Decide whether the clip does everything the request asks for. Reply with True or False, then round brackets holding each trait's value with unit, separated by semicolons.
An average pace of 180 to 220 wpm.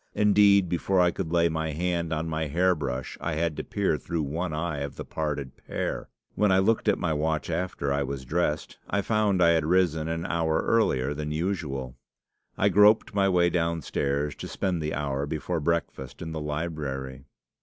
True (190 wpm)